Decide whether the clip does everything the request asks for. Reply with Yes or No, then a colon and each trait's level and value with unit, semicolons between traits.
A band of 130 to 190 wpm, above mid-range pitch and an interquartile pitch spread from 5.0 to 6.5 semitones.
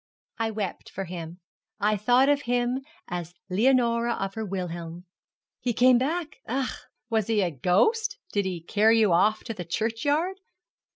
Yes: average, 160 wpm; high, 220 Hz; average, 5.3 semitones